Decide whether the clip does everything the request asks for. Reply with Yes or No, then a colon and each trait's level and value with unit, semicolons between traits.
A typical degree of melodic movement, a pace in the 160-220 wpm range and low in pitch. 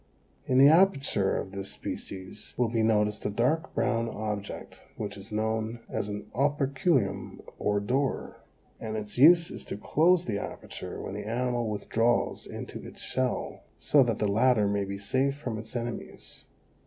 Yes: average, 4.1 semitones; average, 165 wpm; low, 115 Hz